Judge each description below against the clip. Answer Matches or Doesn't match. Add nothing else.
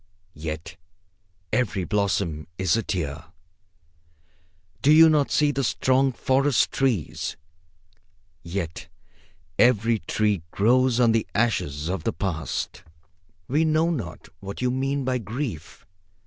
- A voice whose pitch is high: Doesn't match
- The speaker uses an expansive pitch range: Matches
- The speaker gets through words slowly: Matches